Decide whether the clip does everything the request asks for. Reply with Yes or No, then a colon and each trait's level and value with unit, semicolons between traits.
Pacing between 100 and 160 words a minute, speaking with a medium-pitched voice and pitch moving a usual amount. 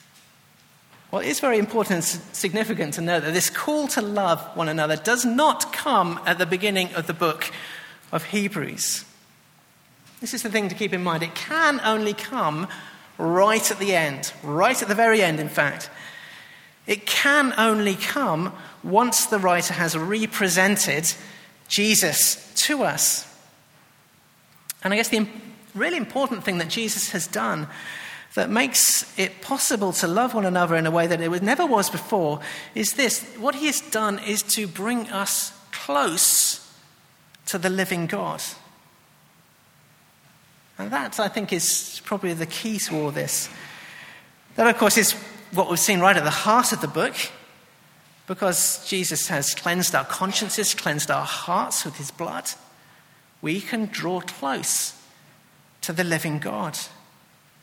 No: average, 155 wpm; high, 195 Hz; average, 4.4 semitones